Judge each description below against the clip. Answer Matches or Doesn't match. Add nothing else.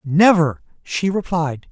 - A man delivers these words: Matches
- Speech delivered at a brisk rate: Doesn't match